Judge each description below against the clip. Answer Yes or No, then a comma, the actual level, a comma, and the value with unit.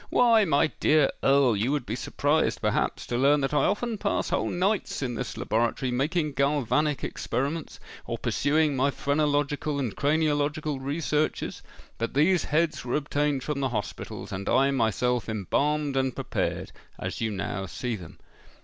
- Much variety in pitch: No, average, 3.3 semitones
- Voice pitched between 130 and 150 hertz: Yes, medium, 140 Hz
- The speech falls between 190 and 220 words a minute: No, average, 160 wpm